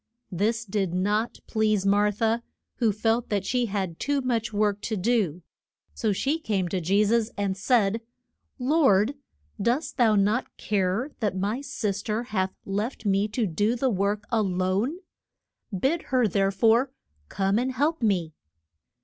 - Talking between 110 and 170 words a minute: Yes, average, 160 wpm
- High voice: Yes, high, 210 Hz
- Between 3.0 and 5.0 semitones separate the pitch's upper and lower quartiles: Yes, average, 3.3 semitones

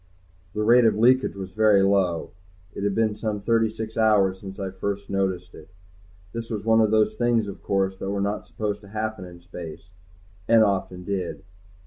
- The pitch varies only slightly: Yes, narrow, 2.3 semitones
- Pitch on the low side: Yes, low, 100 Hz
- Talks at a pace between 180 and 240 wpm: Yes, average, 190 wpm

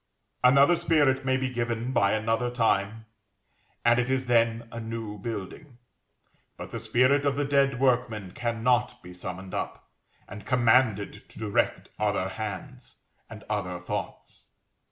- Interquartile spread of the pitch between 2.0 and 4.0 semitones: Yes, average, 3.5 semitones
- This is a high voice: No, low, 115 Hz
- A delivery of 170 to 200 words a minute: No, average, 140 wpm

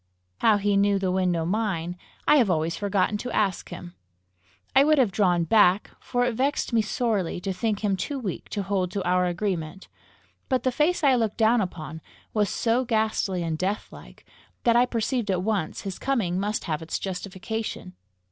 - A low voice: No, high, 200 Hz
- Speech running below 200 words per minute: Yes, average, 185 wpm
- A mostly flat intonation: No, average, 4.0 semitones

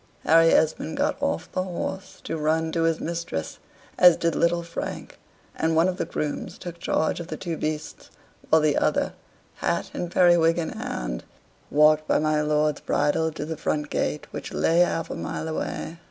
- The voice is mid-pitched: Yes, medium, 160 Hz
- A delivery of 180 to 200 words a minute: Yes, average, 185 wpm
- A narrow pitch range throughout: Yes, narrow, 1.9 semitones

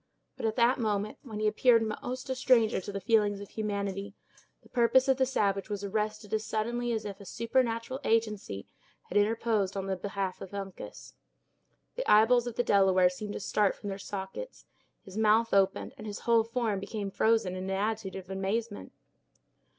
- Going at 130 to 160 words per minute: No, average, 185 wpm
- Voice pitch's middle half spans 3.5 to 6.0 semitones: No, narrow, 2.6 semitones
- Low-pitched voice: No, high, 210 Hz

